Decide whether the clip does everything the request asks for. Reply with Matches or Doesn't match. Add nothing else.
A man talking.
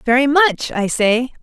Doesn't match